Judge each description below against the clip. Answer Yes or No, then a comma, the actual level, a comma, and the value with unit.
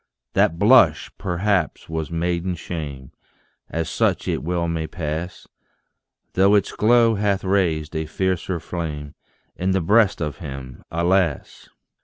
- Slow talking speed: Yes, slow, 130 wpm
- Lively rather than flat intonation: No, average, 3.2 semitones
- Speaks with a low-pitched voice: Yes, very low, 85 Hz